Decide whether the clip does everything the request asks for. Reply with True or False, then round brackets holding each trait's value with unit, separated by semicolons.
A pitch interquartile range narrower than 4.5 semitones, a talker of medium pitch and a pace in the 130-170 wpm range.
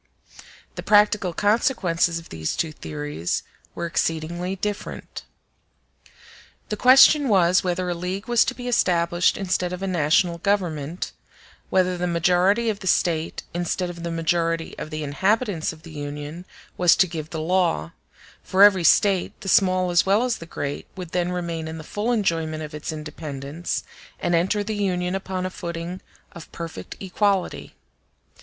True (2.9 semitones; 175 Hz; 160 wpm)